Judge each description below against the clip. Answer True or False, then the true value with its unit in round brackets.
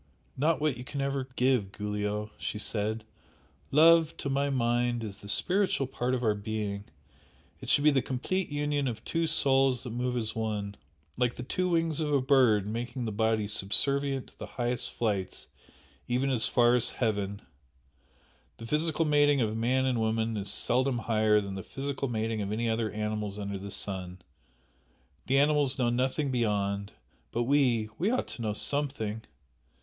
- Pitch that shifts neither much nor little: True (4.4 semitones)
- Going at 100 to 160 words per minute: False (175 wpm)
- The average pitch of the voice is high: False (120 Hz)